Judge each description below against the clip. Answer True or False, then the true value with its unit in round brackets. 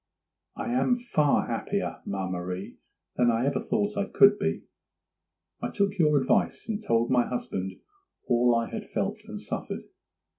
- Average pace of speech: True (155 wpm)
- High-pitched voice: False (135 Hz)